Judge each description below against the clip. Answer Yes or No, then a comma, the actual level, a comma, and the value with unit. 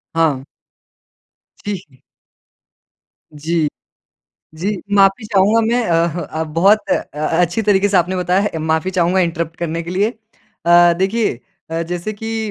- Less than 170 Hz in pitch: No, medium, 180 Hz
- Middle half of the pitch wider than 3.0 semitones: Yes, average, 3.7 semitones